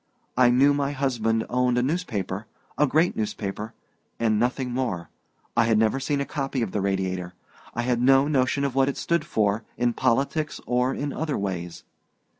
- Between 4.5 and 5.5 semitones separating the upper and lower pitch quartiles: No, average, 4.1 semitones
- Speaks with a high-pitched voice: No, low, 125 Hz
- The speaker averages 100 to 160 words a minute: No, average, 175 wpm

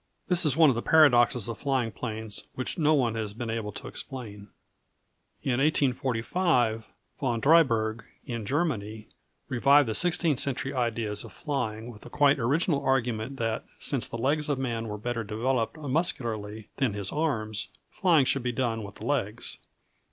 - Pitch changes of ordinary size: Yes, average, 4.2 semitones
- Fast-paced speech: No, average, 165 wpm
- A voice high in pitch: No, low, 120 Hz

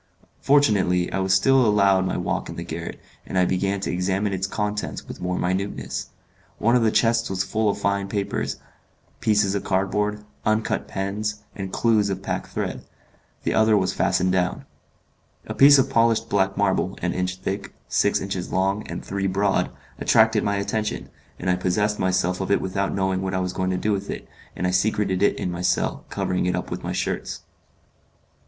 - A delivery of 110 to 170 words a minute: No, average, 190 wpm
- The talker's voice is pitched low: Yes, low, 100 Hz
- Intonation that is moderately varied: No, narrow, 2.1 semitones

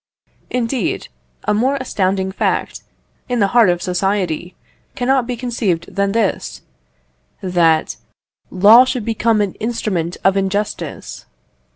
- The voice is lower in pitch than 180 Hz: No, high, 205 Hz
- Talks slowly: Yes, slow, 125 wpm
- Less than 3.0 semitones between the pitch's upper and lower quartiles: No, average, 4.1 semitones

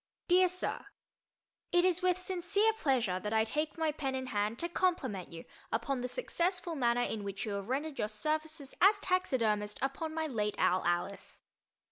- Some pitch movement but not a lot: No, wide, 8.5 semitones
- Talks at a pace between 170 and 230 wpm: Yes, average, 175 wpm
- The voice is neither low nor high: No, very high, 275 Hz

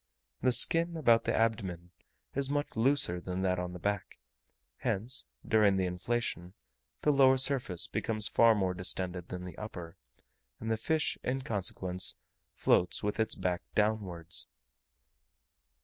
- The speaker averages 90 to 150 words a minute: Yes, average, 140 wpm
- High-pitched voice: No, low, 105 Hz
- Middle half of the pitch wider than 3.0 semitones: Yes, average, 4.8 semitones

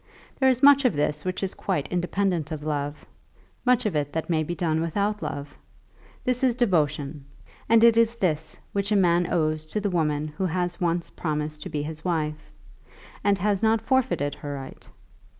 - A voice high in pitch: No, medium, 175 Hz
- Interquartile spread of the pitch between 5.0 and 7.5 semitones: Yes, average, 5.3 semitones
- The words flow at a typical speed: Yes, average, 185 wpm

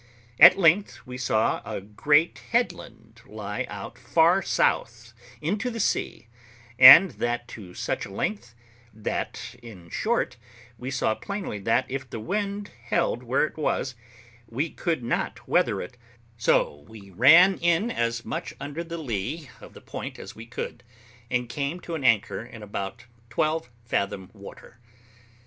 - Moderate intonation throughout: No, wide, 6.8 semitones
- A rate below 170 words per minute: Yes, average, 150 wpm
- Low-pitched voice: Yes, low, 125 Hz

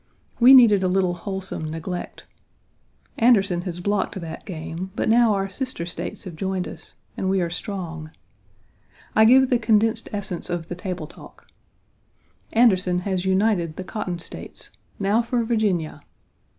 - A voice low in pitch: No, high, 190 Hz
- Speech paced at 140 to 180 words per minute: Yes, average, 150 wpm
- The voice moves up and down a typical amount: Yes, average, 3.8 semitones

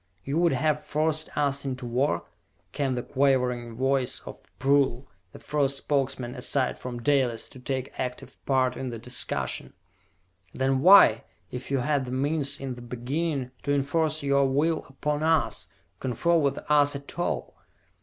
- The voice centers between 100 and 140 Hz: Yes, low, 135 Hz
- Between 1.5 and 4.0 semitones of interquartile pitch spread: Yes, narrow, 2.5 semitones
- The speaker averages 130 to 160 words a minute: Yes, average, 155 wpm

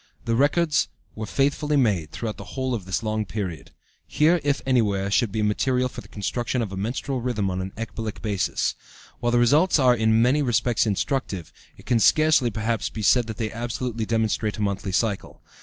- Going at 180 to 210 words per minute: Yes, average, 190 wpm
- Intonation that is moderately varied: Yes, average, 3.4 semitones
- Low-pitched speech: Yes, low, 115 Hz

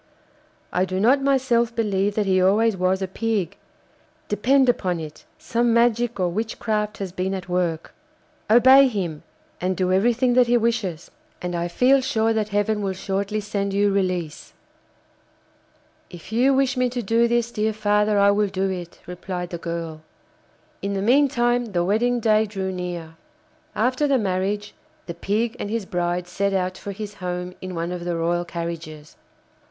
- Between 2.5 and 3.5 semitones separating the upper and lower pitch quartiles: No, average, 4.3 semitones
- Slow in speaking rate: No, average, 170 wpm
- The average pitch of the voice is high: Yes, high, 200 Hz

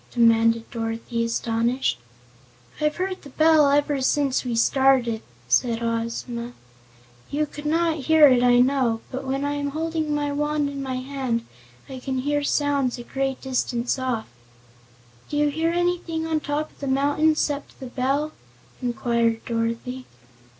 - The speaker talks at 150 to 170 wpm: Yes, average, 155 wpm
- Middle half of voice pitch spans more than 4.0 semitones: No, average, 3.7 semitones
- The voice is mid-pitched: No, very high, 270 Hz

